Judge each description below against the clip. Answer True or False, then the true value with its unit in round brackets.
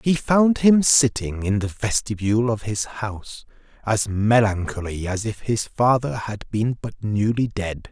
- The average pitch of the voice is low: True (110 Hz)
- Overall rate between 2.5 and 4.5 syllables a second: True (4.2 syllables/s)